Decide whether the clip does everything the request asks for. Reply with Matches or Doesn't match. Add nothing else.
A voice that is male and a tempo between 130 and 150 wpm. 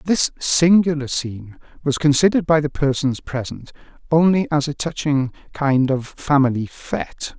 Matches